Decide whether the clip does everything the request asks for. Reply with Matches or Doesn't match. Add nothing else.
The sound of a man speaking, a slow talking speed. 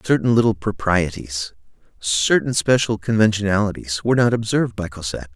Matches